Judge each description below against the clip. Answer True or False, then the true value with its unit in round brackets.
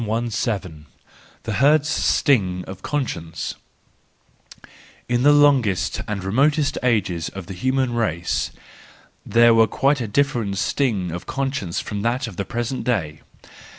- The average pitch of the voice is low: True (115 Hz)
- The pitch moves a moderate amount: False (5.7 semitones)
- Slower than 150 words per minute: True (135 wpm)